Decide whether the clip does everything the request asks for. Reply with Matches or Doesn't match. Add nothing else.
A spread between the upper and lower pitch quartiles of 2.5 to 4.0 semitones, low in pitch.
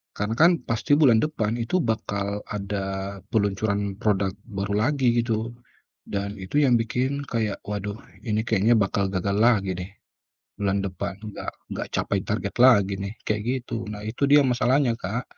Matches